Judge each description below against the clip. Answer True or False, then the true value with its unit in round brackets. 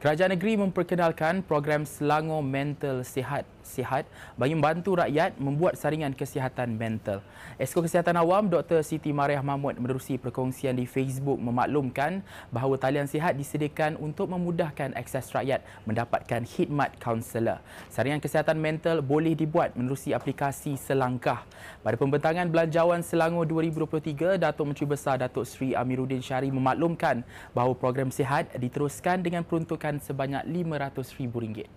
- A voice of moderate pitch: True (145 Hz)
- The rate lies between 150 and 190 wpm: False (125 wpm)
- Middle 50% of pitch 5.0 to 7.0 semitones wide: False (3.7 semitones)